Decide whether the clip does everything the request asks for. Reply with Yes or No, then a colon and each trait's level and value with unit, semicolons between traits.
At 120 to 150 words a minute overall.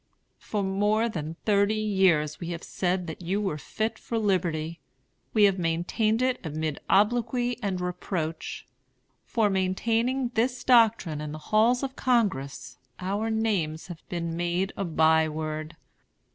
Yes: average, 145 wpm